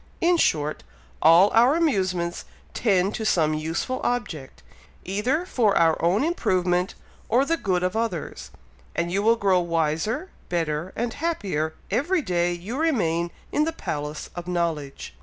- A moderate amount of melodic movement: No, wide, 6.3 semitones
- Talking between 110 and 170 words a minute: Yes, average, 145 wpm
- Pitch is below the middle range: No, medium, 185 Hz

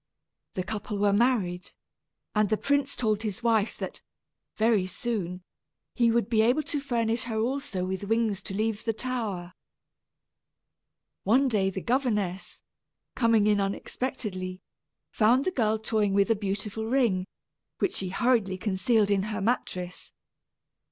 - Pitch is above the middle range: Yes, high, 215 Hz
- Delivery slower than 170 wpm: Yes, average, 140 wpm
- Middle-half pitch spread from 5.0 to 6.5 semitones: No, average, 3.3 semitones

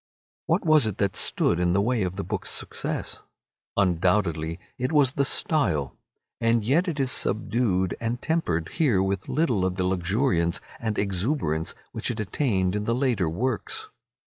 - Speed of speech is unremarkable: Yes, average, 165 wpm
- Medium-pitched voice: No, low, 105 Hz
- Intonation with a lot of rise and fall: Yes, wide, 6.0 semitones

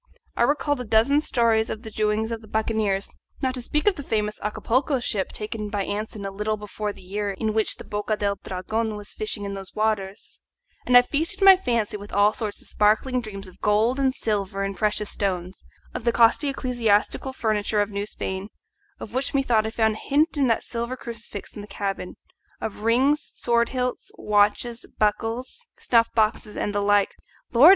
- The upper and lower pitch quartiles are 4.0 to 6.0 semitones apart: No, average, 2.8 semitones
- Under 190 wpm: No, average, 195 wpm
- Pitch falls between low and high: No, high, 220 Hz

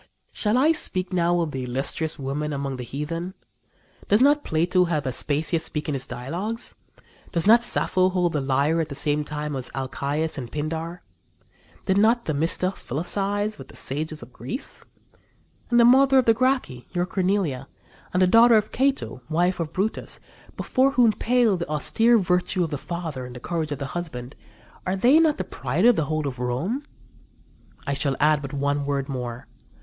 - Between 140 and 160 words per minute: No, average, 185 wpm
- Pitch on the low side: No, medium, 165 Hz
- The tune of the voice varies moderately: No, wide, 6.3 semitones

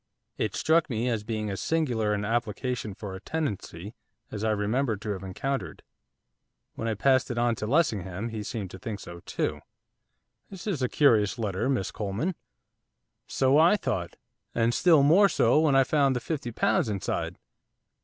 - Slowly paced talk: No, average, 175 wpm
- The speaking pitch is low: Yes, low, 115 Hz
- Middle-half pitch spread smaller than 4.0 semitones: No, average, 5.0 semitones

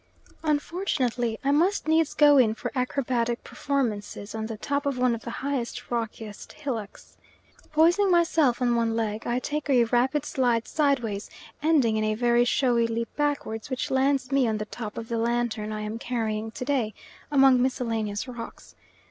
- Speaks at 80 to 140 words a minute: No, average, 170 wpm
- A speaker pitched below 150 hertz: No, high, 245 Hz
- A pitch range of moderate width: Yes, average, 3.8 semitones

